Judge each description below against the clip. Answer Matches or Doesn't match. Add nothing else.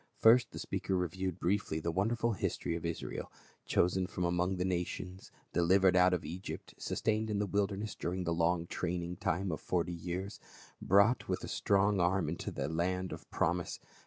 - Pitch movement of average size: Doesn't match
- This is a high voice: Doesn't match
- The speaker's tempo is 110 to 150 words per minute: Doesn't match